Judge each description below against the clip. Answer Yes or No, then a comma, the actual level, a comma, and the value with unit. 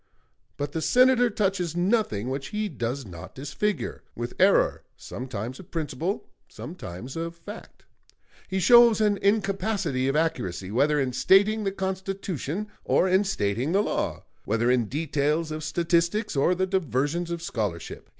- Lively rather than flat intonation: Yes, wide, 6.8 semitones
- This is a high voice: No, medium, 165 Hz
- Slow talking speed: No, average, 145 wpm